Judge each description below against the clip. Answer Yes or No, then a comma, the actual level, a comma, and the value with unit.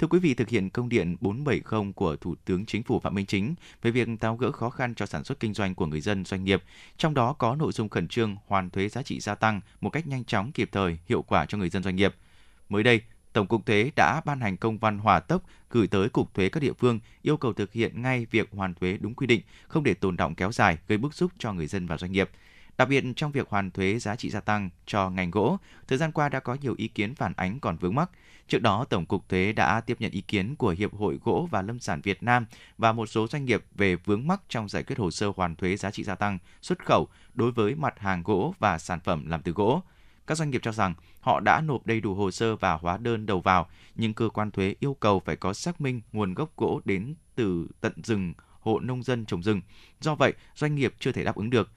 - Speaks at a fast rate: Yes, fast, 265 wpm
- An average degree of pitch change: Yes, average, 4.0 semitones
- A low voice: Yes, low, 105 Hz